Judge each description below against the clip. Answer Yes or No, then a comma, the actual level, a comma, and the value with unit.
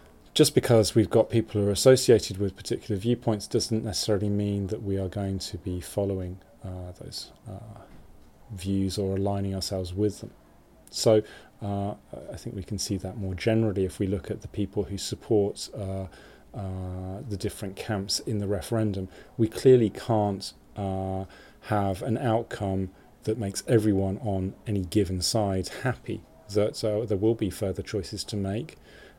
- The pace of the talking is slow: No, average, 160 wpm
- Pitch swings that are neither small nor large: No, narrow, 2.3 semitones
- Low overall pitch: Yes, low, 100 Hz